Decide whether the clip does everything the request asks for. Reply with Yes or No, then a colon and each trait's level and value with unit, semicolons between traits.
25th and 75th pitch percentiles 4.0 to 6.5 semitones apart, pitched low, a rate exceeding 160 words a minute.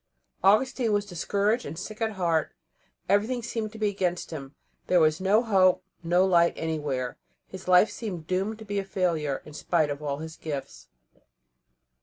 No: average, 4.7 semitones; medium, 185 Hz; average, 170 wpm